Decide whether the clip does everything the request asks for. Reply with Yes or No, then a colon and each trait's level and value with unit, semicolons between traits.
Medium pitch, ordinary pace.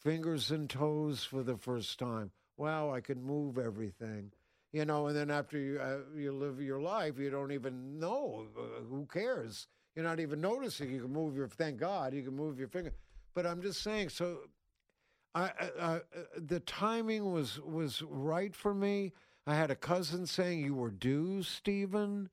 Yes: medium, 150 Hz; average, 185 wpm